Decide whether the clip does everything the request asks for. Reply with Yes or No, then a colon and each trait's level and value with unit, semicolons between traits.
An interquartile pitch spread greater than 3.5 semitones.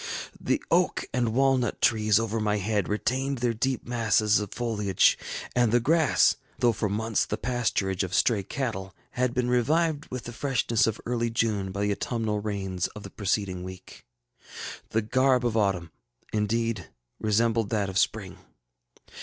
No: average, 3.0 semitones